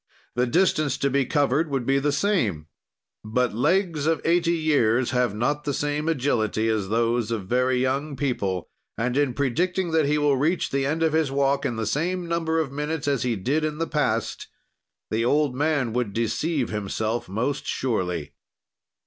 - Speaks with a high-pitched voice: No, medium, 140 Hz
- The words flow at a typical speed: Yes, average, 180 wpm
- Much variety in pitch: No, average, 4.7 semitones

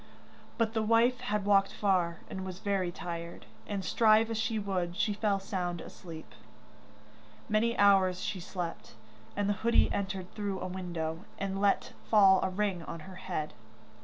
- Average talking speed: Yes, average, 165 wpm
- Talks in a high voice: Yes, high, 195 Hz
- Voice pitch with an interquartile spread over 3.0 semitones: No, average, 2.7 semitones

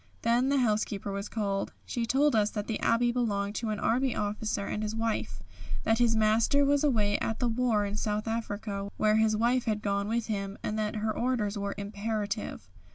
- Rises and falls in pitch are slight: Yes, narrow, 2.2 semitones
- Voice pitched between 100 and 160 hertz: No, high, 215 Hz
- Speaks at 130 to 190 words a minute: No, average, 200 wpm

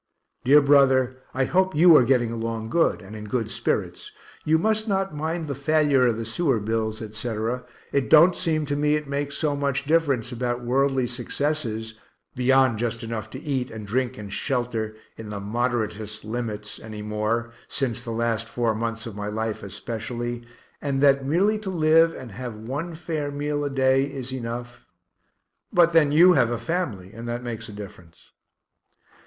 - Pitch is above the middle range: No, low, 125 Hz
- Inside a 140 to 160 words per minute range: No, average, 175 wpm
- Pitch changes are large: No, average, 4.5 semitones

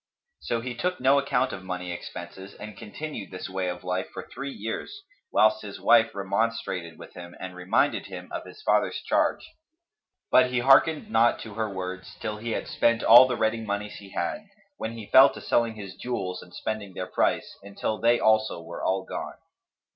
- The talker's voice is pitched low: Yes, low, 110 Hz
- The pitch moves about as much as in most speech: Yes, average, 4.2 semitones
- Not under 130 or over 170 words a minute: No, average, 190 wpm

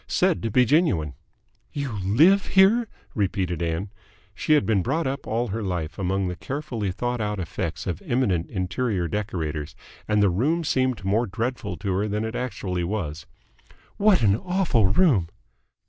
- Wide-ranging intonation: Yes, wide, 6.0 semitones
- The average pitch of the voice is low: Yes, low, 105 Hz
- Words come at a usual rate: Yes, average, 160 wpm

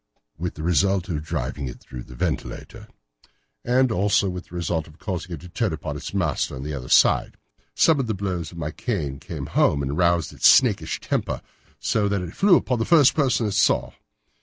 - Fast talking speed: Yes, fast, 210 wpm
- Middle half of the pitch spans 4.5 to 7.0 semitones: Yes, average, 5.2 semitones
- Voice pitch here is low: Yes, very low, 90 Hz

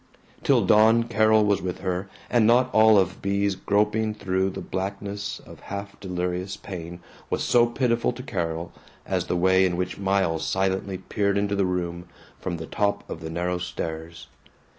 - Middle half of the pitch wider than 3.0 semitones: No, narrow, 2.5 semitones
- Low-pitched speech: Yes, very low, 95 Hz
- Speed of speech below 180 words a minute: Yes, average, 170 wpm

